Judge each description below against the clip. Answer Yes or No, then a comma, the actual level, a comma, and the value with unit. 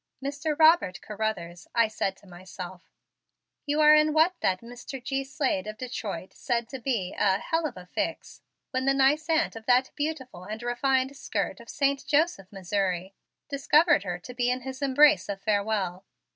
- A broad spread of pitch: Yes, wide, 6.4 semitones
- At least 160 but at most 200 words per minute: Yes, average, 175 wpm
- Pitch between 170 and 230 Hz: No, high, 245 Hz